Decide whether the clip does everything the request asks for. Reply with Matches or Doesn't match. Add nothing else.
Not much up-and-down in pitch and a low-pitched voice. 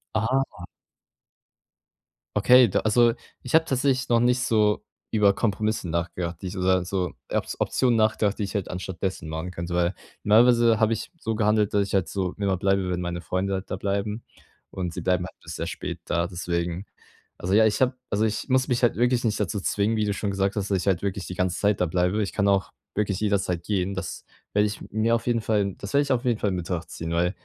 Doesn't match